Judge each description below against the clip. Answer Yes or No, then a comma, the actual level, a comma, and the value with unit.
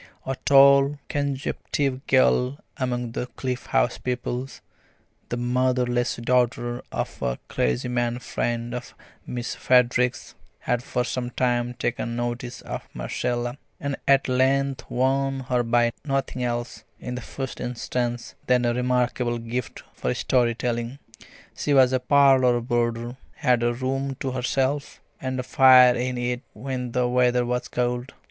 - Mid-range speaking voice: No, low, 125 Hz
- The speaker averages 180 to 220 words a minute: No, average, 140 wpm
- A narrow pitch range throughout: Yes, narrow, 1.4 semitones